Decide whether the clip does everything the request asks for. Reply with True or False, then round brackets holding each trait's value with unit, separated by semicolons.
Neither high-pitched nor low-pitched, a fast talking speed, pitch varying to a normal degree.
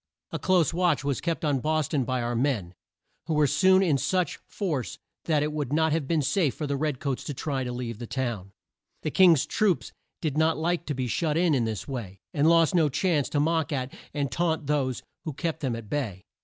True (145 Hz; 225 wpm; 3.9 semitones)